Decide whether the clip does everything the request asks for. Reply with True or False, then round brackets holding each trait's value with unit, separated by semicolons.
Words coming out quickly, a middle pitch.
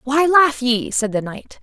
False (220 wpm; 255 Hz)